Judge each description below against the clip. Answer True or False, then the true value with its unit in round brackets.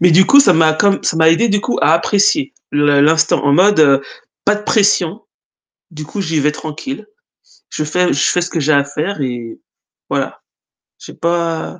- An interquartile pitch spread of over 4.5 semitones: True (4.9 semitones)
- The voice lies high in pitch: False (165 Hz)